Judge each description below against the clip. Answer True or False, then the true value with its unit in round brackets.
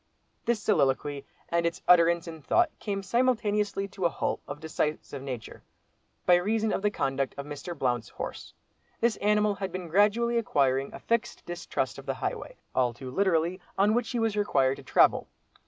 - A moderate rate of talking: True (170 wpm)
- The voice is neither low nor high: True (180 Hz)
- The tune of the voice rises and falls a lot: True (6.4 semitones)